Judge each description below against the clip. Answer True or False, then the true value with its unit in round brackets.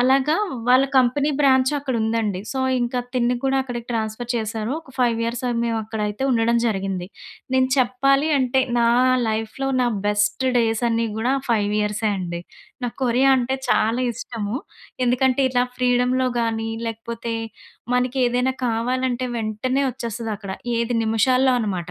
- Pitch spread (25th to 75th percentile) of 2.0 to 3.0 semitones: True (2.6 semitones)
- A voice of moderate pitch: False (240 Hz)